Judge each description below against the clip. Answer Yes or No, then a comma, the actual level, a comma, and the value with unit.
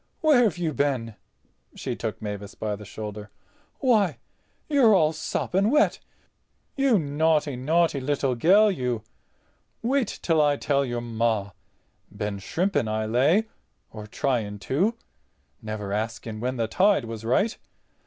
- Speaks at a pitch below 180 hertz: Yes, low, 135 Hz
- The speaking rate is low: Yes, slow, 125 wpm